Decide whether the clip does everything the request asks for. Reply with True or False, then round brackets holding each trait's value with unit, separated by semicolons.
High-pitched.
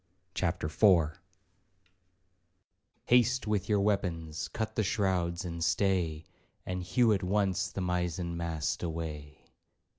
False (90 Hz)